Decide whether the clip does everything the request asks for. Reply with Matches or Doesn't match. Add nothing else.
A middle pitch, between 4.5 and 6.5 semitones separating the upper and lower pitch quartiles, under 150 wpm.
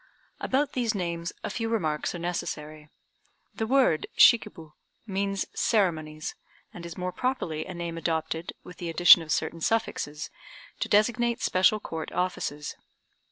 Matches